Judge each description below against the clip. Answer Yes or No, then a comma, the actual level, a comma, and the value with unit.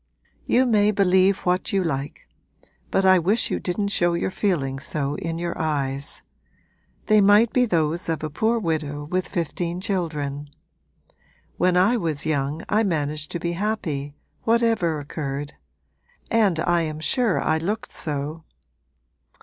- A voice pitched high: No, medium, 170 Hz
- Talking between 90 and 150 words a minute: Yes, average, 145 wpm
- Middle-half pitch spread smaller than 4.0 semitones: No, average, 4.8 semitones